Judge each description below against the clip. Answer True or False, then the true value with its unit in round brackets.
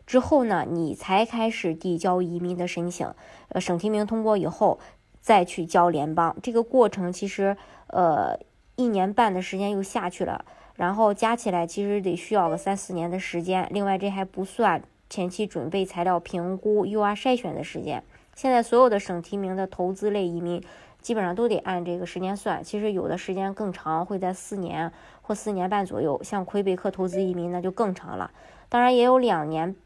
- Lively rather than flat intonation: False (2.9 semitones)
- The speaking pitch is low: False (190 Hz)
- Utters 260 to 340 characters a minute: True (290 characters per minute)